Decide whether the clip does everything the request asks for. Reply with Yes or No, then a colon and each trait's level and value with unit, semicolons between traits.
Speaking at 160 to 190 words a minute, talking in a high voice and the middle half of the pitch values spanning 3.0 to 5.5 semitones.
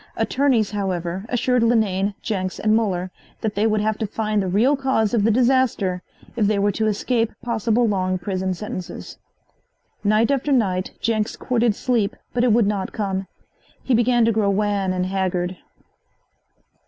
Yes: average, 165 wpm; high, 215 Hz; average, 3.3 semitones